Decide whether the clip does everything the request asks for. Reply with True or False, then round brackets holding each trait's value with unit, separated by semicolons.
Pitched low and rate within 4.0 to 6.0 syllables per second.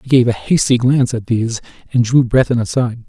False (120 Hz; 6.4 syllables/s)